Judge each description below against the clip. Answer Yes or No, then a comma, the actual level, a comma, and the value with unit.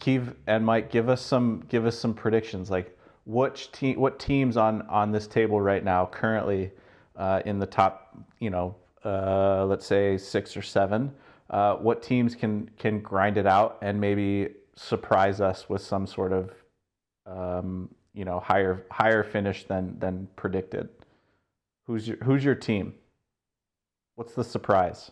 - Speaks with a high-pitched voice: No, low, 100 Hz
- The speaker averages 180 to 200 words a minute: No, average, 160 wpm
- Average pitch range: Yes, average, 3.0 semitones